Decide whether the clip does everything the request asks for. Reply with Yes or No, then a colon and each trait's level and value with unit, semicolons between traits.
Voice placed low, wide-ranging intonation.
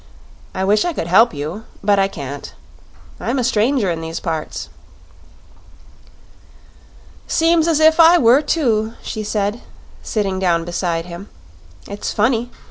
No: high, 210 Hz; wide, 6.3 semitones